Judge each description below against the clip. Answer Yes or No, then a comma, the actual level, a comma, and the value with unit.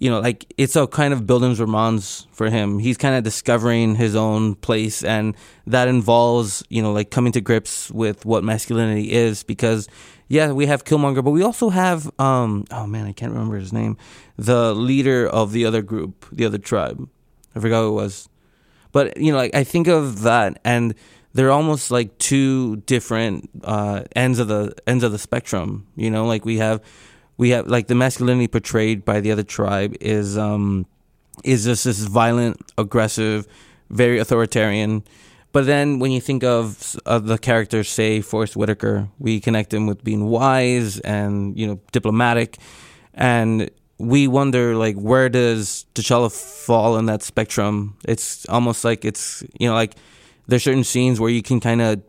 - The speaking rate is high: No, average, 180 wpm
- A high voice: No, low, 115 Hz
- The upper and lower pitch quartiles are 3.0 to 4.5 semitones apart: No, narrow, 2.6 semitones